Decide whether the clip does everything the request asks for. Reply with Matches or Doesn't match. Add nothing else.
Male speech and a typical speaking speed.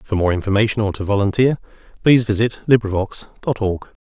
Matches